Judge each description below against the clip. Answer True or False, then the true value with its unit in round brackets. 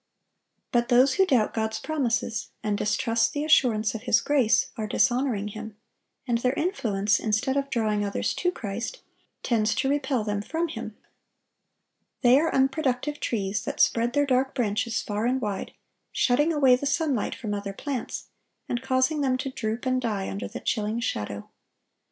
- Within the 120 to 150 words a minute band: False (165 wpm)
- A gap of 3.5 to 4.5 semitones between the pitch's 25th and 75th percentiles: True (4.0 semitones)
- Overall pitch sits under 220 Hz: False (240 Hz)